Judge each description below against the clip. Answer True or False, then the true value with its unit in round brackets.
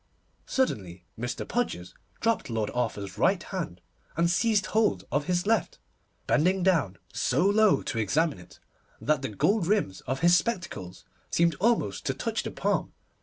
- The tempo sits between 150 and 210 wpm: True (155 wpm)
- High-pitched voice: False (165 Hz)